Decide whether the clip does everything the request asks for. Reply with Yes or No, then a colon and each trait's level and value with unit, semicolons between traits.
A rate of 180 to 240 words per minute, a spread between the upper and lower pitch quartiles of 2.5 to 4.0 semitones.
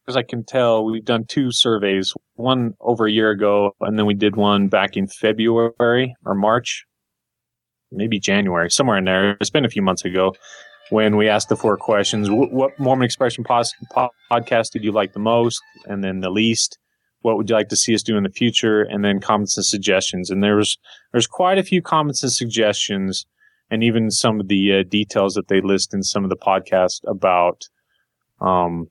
Yes: average, 200 wpm; average, 2.9 semitones